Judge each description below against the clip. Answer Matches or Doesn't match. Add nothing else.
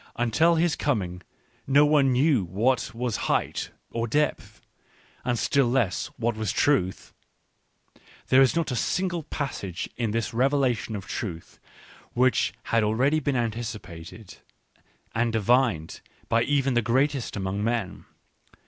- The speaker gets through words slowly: Matches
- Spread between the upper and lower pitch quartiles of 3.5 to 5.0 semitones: Matches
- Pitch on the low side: Matches